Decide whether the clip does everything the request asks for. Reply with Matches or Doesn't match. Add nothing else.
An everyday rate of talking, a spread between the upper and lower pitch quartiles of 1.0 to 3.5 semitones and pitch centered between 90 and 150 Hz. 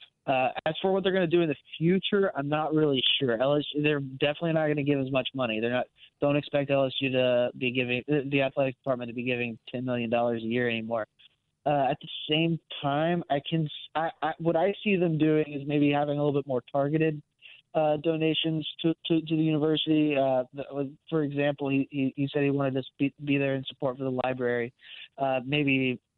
Doesn't match